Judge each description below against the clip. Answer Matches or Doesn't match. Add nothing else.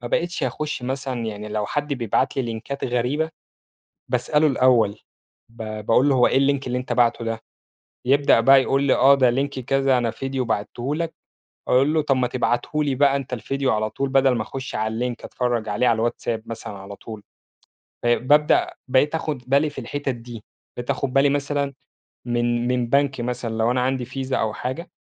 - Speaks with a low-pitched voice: Matches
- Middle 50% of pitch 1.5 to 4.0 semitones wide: Matches